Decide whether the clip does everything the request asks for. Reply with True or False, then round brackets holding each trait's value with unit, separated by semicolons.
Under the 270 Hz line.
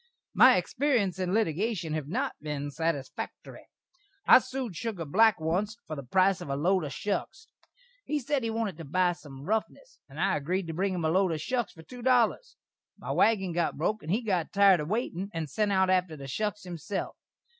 True (185 Hz)